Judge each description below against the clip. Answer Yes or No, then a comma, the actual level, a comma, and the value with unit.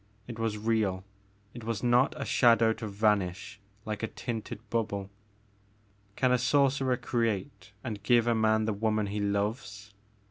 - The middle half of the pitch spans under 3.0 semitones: Yes, narrow, 2.5 semitones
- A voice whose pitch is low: Yes, low, 110 Hz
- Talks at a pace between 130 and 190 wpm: Yes, average, 155 wpm